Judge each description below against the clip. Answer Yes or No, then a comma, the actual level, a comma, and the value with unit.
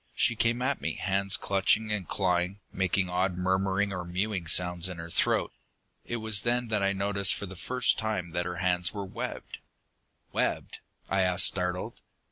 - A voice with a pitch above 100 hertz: No, very low, 95 Hz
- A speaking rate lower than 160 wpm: No, average, 175 wpm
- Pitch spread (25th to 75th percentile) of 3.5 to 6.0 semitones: No, narrow, 2.4 semitones